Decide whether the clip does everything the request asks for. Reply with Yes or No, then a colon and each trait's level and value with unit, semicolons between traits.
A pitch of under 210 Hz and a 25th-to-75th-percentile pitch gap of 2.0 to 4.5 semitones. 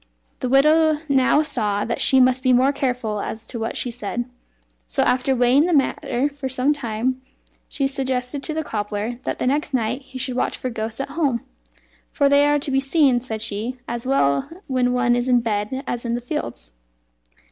No: very high, 255 Hz; average, 2.7 semitones